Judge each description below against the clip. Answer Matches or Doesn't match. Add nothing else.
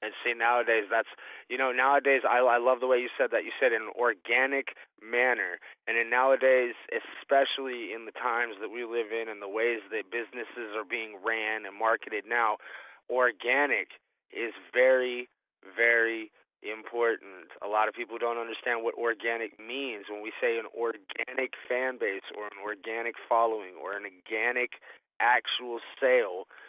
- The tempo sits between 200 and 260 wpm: Doesn't match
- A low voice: Matches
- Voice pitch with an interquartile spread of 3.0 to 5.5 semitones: Doesn't match